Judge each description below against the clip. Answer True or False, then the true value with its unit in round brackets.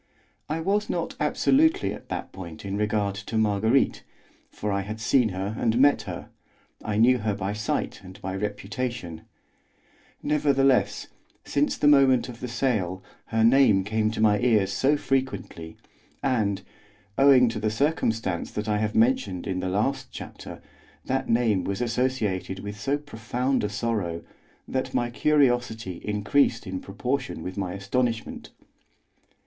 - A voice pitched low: True (110 Hz)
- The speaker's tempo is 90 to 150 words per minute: True (145 wpm)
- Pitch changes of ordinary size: True (4.5 semitones)